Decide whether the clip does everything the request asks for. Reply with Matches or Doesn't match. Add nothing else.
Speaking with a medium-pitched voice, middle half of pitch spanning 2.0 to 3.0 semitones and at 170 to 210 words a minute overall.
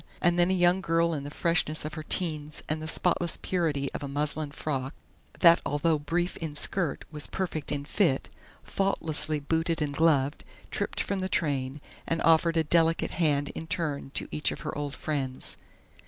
Matches